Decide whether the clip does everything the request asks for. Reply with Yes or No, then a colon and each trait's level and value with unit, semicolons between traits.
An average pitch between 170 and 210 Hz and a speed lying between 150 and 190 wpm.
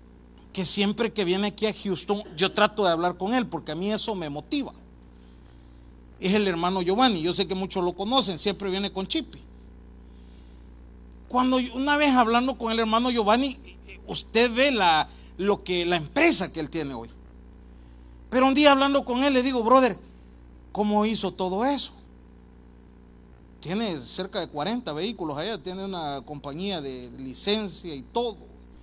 Yes: high, 190 Hz; average, 160 wpm